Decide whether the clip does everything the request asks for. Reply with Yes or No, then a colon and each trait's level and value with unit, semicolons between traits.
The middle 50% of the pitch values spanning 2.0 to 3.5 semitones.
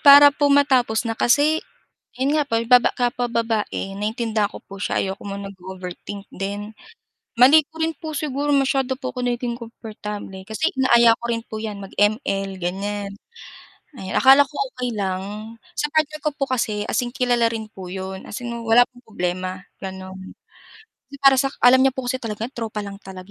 No: average, 4.7 semitones